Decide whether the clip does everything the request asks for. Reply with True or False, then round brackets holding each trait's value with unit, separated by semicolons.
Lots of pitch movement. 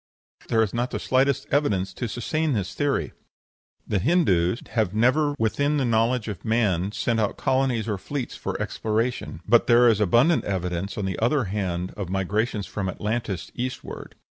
False (4.5 semitones)